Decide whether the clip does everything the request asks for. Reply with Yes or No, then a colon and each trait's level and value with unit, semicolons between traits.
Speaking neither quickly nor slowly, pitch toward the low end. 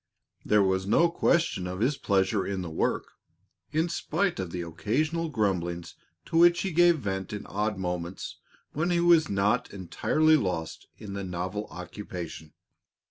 Yes: average, 155 wpm; low, 100 Hz